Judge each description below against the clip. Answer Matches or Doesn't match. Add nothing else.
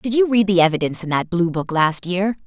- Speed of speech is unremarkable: Doesn't match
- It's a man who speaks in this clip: Doesn't match